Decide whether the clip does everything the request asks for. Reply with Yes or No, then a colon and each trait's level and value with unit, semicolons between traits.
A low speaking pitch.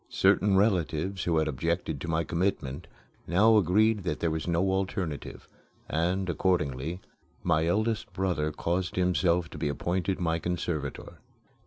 Yes: very low, 85 Hz